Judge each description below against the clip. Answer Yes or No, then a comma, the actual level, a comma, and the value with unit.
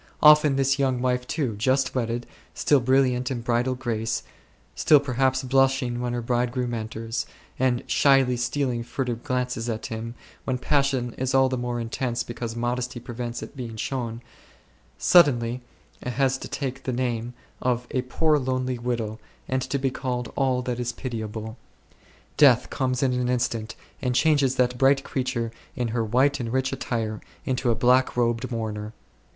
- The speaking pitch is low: Yes, low, 125 Hz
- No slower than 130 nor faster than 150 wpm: No, average, 160 wpm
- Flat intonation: Yes, narrow, 1.8 semitones